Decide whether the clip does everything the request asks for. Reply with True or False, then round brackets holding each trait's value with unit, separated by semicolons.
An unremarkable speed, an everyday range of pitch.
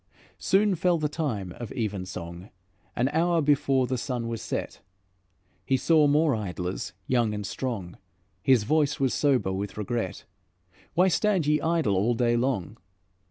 False (150 wpm; 6.5 semitones)